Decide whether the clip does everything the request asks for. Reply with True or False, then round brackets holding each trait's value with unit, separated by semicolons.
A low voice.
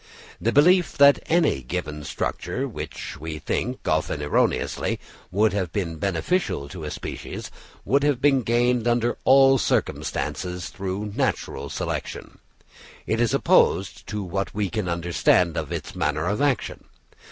True (105 Hz)